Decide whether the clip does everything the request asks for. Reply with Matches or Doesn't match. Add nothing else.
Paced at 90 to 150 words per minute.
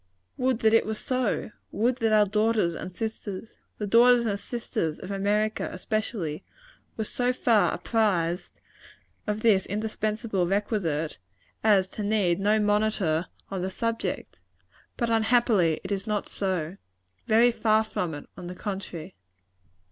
Matches